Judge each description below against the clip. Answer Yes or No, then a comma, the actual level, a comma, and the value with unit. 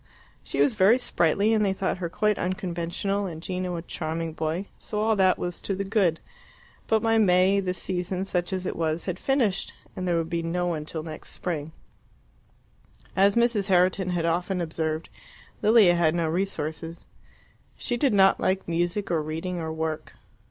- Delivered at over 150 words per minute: Yes, average, 180 wpm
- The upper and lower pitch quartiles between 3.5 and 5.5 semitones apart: No, average, 3.0 semitones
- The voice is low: No, medium, 180 Hz